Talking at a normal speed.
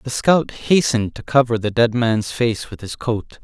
No: fast, 210 wpm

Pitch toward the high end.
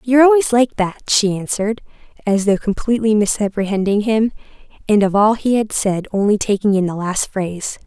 Yes: high, 210 Hz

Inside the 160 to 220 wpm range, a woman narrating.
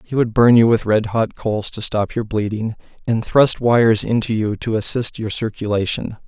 No: average, 200 wpm; male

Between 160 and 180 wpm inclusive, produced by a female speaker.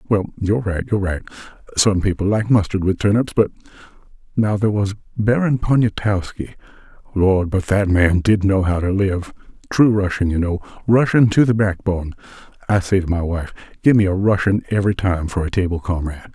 No: average, 175 wpm; male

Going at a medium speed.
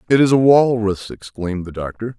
Yes: average, 190 wpm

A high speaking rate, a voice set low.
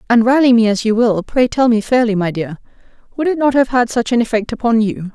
No: fast, 255 wpm; high, 230 Hz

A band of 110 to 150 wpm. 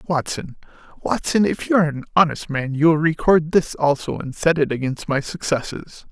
No: average, 185 wpm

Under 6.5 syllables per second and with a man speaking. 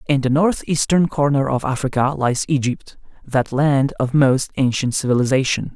Yes: 4.8 syllables/s; male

